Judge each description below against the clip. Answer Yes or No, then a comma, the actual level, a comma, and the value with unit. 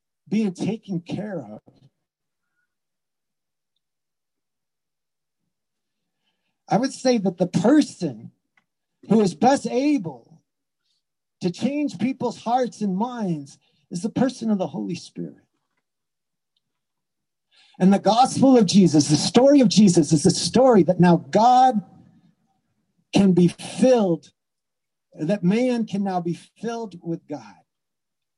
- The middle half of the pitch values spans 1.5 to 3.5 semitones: No, average, 5.3 semitones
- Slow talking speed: Yes, slow, 110 wpm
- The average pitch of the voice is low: No, high, 200 Hz